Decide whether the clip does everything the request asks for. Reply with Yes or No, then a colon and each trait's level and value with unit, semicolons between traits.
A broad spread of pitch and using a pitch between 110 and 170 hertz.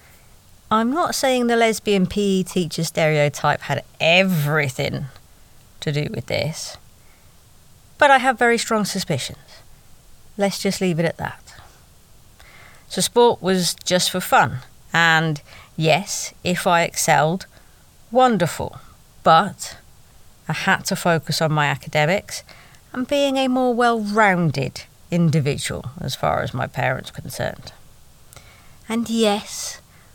No: wide, 6.1 semitones; medium, 180 Hz